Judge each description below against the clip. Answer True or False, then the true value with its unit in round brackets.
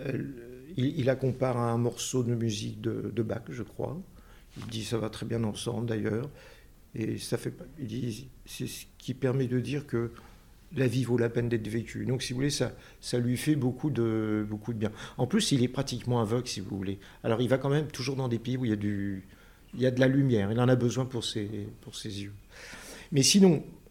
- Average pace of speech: False (235 wpm)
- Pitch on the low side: True (120 Hz)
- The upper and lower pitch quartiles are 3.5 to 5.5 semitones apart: False (2.9 semitones)